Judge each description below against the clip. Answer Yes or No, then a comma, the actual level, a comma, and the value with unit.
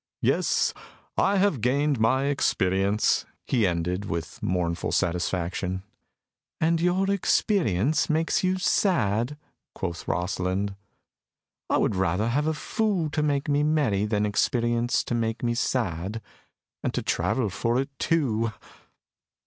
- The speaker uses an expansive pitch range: Yes, wide, 7.5 semitones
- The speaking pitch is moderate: No, low, 115 Hz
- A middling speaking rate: No, slow, 125 wpm